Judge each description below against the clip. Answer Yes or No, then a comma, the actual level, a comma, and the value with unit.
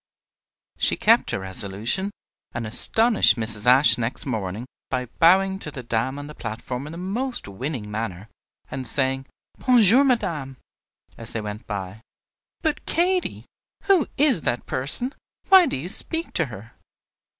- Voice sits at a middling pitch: No, low, 130 Hz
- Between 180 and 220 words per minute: No, average, 150 wpm